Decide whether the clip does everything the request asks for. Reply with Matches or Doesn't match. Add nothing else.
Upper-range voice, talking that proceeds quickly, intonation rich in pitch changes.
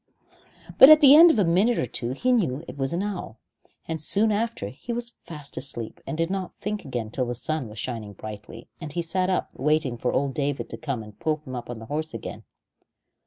Doesn't match